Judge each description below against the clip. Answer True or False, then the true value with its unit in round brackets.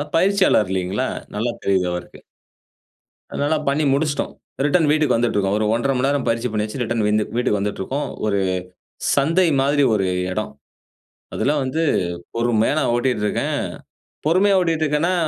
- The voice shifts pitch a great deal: True (6.0 semitones)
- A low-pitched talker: True (130 Hz)